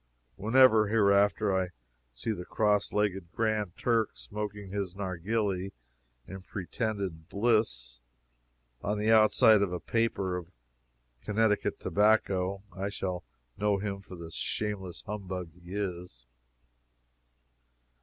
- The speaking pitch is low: Yes, low, 100 Hz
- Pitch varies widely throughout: No, narrow, 2.6 semitones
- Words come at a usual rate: No, slow, 115 wpm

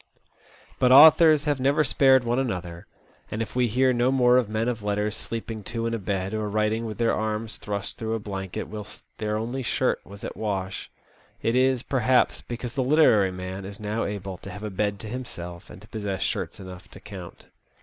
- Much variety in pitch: No, average, 3.5 semitones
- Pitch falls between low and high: No, low, 110 Hz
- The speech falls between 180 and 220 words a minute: Yes, fast, 205 wpm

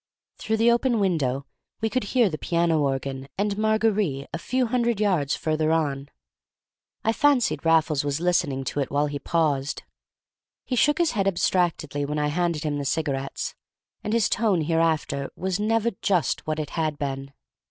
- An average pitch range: No, wide, 6.6 semitones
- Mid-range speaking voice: Yes, medium, 165 Hz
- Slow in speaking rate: No, average, 170 wpm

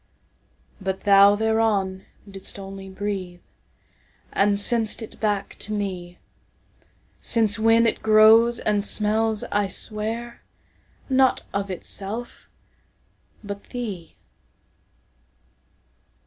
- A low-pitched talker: No, high, 205 Hz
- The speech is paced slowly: Yes, slow, 80 wpm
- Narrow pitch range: Yes, narrow, 2.2 semitones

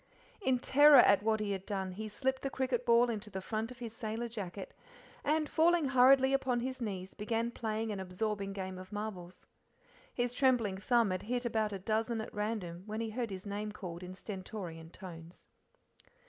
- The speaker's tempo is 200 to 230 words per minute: No, average, 190 wpm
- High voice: Yes, high, 215 Hz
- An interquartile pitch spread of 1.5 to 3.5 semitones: No, average, 4.0 semitones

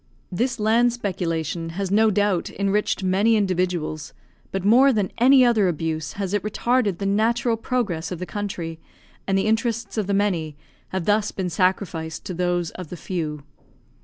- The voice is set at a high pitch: Yes, high, 195 Hz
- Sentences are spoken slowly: No, average, 165 wpm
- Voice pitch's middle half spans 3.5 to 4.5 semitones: Yes, average, 3.8 semitones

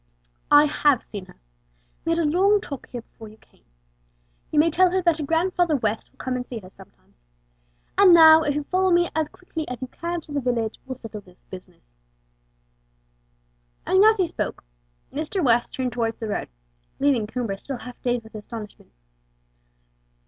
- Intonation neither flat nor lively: No, wide, 6.4 semitones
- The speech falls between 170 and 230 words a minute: Yes, average, 185 wpm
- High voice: Yes, very high, 280 Hz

